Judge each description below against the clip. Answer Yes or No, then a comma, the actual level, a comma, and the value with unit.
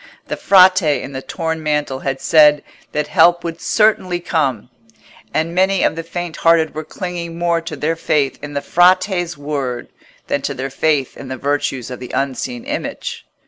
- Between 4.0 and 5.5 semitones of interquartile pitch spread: No, average, 3.6 semitones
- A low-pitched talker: No, medium, 160 Hz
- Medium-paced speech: Yes, average, 180 wpm